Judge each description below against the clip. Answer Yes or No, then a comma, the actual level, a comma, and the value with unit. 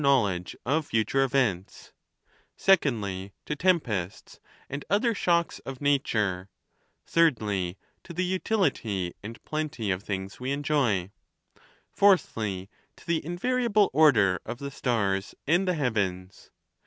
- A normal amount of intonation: No, wide, 8.6 semitones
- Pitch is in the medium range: No, low, 130 Hz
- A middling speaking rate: No, slow, 115 wpm